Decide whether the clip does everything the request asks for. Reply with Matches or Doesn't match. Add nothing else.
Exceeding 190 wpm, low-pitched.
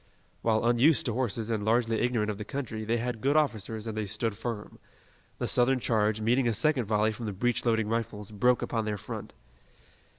Matches